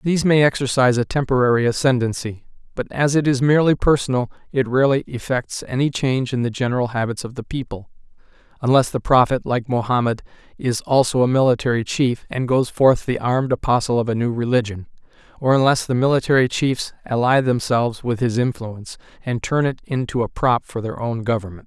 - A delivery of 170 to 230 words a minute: Yes, average, 175 wpm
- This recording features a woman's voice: No, male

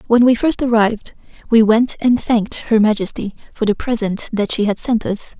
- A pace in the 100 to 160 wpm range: No, average, 200 wpm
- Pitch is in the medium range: No, high, 225 Hz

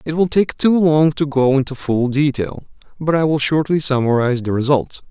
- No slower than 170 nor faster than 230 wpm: Yes, average, 200 wpm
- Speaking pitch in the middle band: Yes, medium, 145 Hz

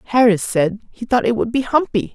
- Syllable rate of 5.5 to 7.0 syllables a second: Yes, 5.6 syllables/s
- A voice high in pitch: Yes, high, 225 Hz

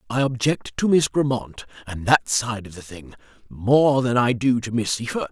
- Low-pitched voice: Yes, low, 120 Hz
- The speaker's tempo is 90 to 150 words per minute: No, fast, 205 wpm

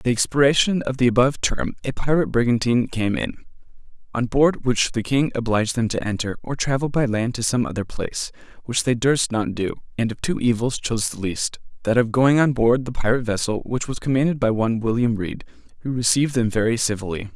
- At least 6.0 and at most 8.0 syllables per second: Yes, 6.1 syllables/s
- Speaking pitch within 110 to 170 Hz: Yes, low, 120 Hz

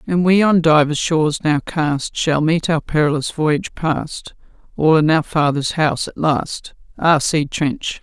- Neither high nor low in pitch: Yes, medium, 155 Hz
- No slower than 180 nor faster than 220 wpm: No, average, 170 wpm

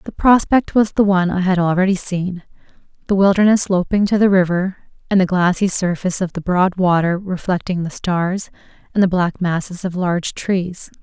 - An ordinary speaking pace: Yes, average, 175 wpm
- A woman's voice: Yes, female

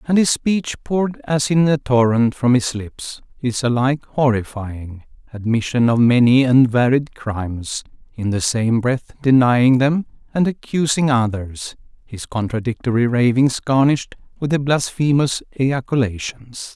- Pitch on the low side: Yes, low, 125 Hz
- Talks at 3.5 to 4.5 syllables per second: Yes, 4.3 syllables/s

